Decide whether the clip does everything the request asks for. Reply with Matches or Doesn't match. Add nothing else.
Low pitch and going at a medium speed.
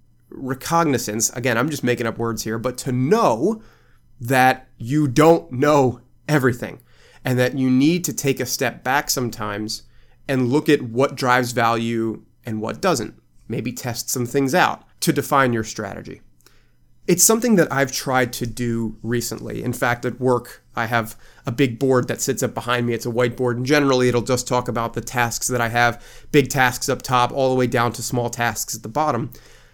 Matches